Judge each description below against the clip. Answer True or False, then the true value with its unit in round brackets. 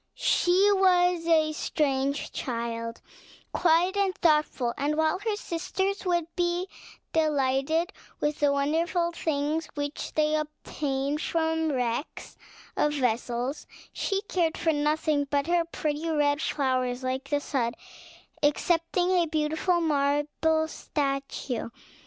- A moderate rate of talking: False (120 wpm)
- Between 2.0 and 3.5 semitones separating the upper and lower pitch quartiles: True (3.2 semitones)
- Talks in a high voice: True (305 Hz)